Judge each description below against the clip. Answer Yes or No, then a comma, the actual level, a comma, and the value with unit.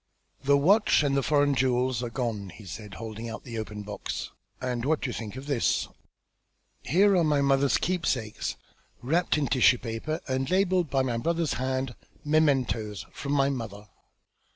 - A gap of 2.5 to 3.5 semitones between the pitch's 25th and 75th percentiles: No, average, 4.2 semitones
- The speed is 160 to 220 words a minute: Yes, average, 170 wpm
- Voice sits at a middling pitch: No, low, 130 Hz